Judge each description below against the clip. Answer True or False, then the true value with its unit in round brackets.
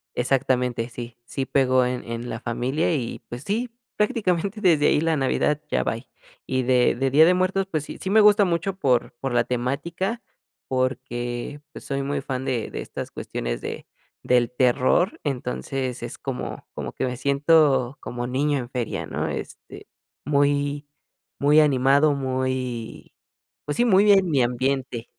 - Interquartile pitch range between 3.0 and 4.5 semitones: True (3.7 semitones)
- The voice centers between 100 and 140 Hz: True (135 Hz)